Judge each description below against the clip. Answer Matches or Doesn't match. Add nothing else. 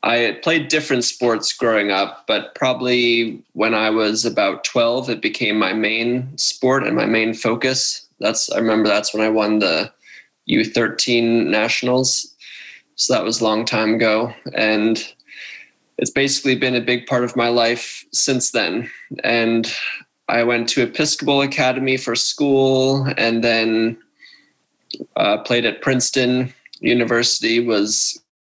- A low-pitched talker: Matches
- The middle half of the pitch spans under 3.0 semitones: Matches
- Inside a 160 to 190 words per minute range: Doesn't match